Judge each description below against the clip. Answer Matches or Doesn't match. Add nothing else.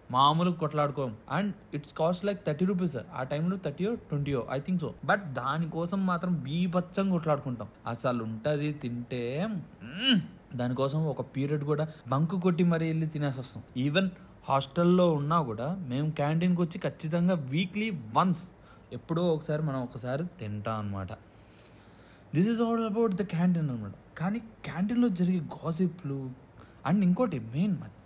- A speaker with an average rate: Doesn't match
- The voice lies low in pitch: Doesn't match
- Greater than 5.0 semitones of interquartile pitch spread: Matches